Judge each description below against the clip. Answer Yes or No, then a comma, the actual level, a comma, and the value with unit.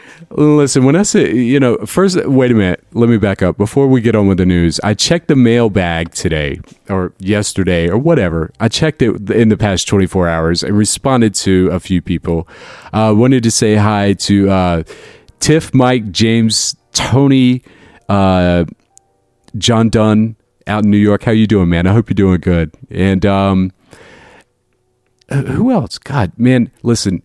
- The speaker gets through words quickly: No, average, 170 wpm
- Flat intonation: No, average, 4.9 semitones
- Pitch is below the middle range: Yes, low, 105 Hz